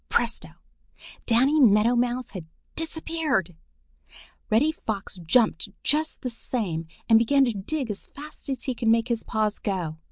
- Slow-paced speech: No, average, 150 wpm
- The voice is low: No, high, 235 Hz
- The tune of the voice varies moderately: Yes, average, 4.8 semitones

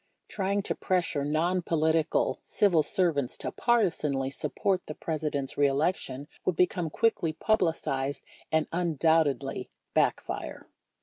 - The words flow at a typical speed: No, slow, 125 wpm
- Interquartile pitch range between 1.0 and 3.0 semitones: No, average, 4.0 semitones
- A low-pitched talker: No, medium, 160 Hz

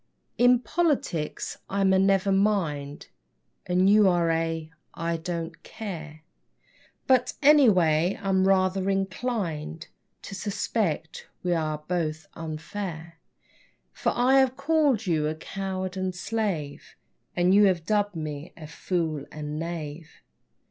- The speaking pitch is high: No, medium, 180 Hz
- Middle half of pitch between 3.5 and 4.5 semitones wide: Yes, average, 4.0 semitones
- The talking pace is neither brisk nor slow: No, slow, 125 wpm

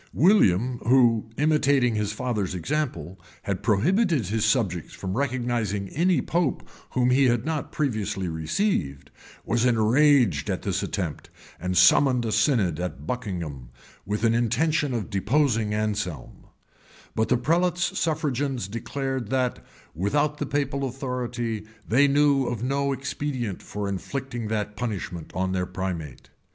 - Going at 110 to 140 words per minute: Yes, slow, 135 wpm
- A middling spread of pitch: No, wide, 5.7 semitones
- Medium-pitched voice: No, low, 120 Hz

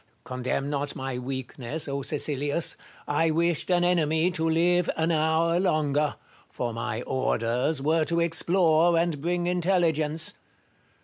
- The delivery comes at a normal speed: No, slow, 130 wpm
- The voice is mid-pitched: Yes, medium, 160 Hz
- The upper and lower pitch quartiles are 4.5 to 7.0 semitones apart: No, average, 3.3 semitones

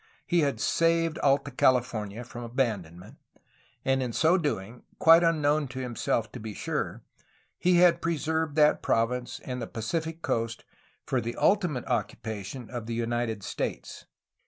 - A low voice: Yes, low, 125 Hz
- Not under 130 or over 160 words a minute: Yes, average, 145 wpm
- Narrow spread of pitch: No, wide, 5.6 semitones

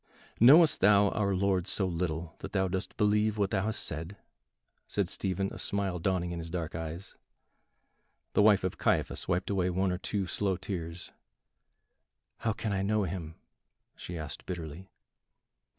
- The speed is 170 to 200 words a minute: No, average, 160 wpm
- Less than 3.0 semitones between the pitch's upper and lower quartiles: Yes, narrow, 2.6 semitones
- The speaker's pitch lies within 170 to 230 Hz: No, very low, 95 Hz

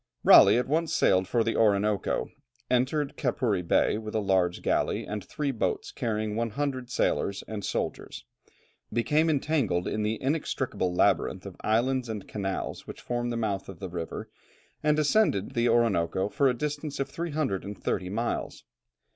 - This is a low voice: Yes, low, 115 Hz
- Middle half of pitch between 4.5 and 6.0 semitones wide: Yes, average, 5.2 semitones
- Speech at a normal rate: Yes, average, 155 wpm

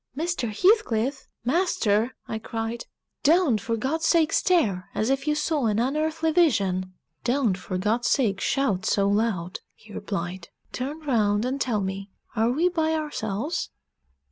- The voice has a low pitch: No, high, 240 Hz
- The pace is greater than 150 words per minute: No, average, 145 wpm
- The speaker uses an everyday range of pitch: No, wide, 6.9 semitones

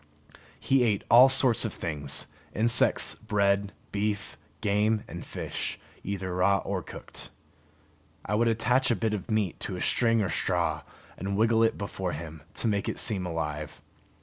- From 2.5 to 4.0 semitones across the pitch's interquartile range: Yes, average, 3.4 semitones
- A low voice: Yes, low, 105 Hz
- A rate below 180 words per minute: Yes, average, 160 wpm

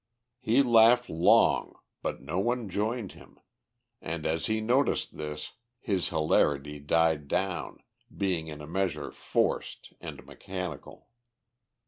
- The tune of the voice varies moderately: No, wide, 6.1 semitones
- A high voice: No, very low, 90 Hz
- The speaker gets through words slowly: Yes, slow, 120 wpm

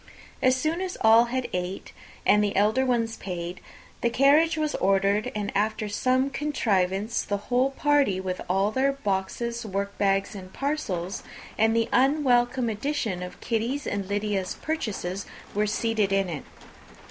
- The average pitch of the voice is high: Yes, high, 220 Hz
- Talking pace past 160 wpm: No, average, 145 wpm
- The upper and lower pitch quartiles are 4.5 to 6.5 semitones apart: Yes, average, 4.8 semitones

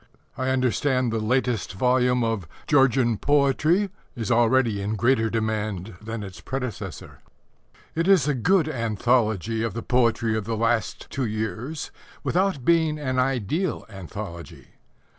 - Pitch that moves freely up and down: No, average, 3.6 semitones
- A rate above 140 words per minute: No, slow, 135 wpm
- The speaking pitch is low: Yes, low, 120 Hz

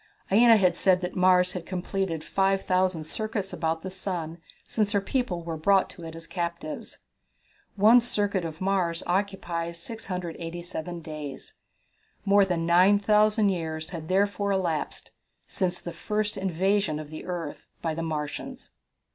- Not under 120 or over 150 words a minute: Yes, average, 140 wpm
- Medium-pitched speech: Yes, medium, 180 Hz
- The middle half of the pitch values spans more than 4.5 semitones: No, average, 3.0 semitones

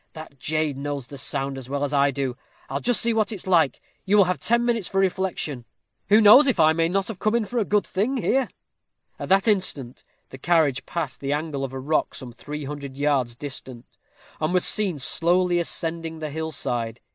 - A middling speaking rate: No, fast, 215 wpm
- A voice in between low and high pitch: Yes, medium, 160 Hz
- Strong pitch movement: Yes, wide, 5.7 semitones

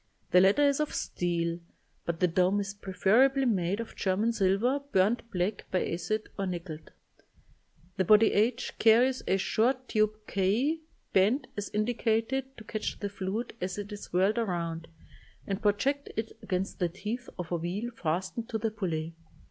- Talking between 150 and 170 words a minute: Yes, average, 165 wpm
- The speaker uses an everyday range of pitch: Yes, average, 3.9 semitones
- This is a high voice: Yes, high, 205 Hz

